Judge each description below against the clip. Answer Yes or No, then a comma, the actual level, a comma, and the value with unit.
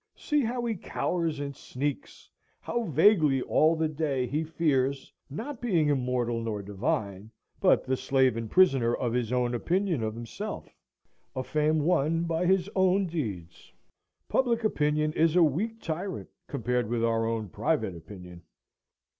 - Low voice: No, medium, 145 Hz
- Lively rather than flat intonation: Yes, wide, 6.1 semitones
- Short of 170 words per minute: Yes, average, 150 wpm